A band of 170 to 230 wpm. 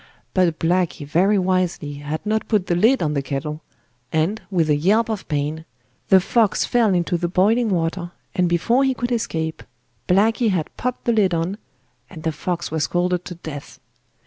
Yes: average, 180 wpm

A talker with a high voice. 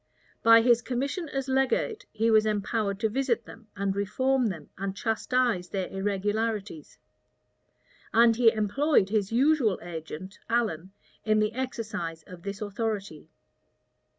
Yes: high, 215 Hz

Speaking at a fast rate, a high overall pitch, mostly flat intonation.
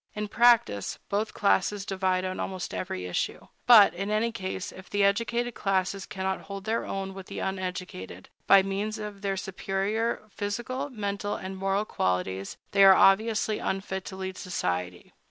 No: average, 160 wpm; high, 195 Hz; narrow, 2.0 semitones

